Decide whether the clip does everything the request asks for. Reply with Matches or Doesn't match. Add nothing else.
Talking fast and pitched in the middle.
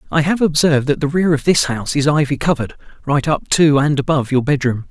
Matches